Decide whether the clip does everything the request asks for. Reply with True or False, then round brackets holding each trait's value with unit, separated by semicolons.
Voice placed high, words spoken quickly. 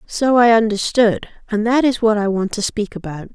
True (215 Hz; 215 wpm)